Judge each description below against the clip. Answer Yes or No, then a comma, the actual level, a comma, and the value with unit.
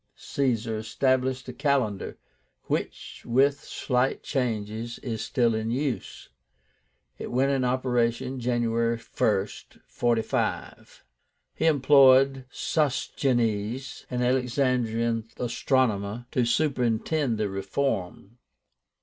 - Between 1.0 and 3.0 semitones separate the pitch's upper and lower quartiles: Yes, average, 2.7 semitones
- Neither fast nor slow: No, slow, 90 wpm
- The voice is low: Yes, low, 125 Hz